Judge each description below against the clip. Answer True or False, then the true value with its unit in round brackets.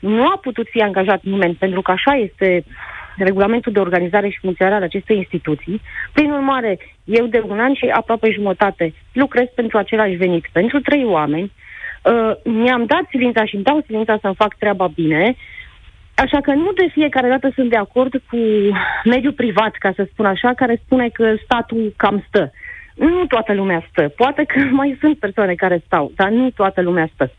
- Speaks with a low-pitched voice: False (220 Hz)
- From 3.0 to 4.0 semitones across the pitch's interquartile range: False (4.7 semitones)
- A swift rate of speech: True (185 wpm)